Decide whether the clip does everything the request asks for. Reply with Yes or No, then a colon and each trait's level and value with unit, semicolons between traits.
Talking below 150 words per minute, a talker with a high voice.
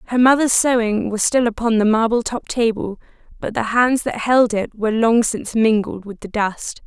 No: average, 200 wpm; high, 225 Hz